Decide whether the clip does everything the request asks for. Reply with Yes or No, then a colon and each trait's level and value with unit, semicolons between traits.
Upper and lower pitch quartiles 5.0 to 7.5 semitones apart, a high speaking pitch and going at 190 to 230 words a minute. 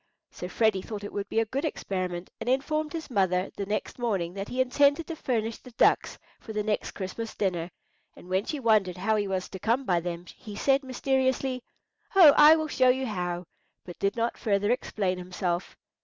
Yes: wide, 5.6 semitones; high, 215 Hz; average, 200 wpm